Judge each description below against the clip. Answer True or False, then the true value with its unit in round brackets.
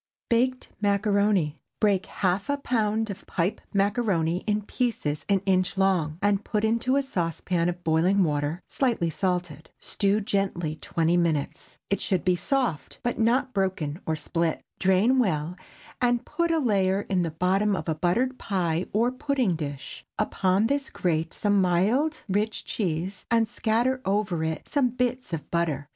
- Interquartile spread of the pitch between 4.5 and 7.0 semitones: True (5.0 semitones)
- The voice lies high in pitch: True (195 Hz)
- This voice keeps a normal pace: True (160 wpm)